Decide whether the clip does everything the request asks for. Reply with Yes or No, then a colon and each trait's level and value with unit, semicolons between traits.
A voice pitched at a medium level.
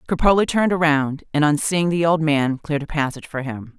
Yes: medium, 155 Hz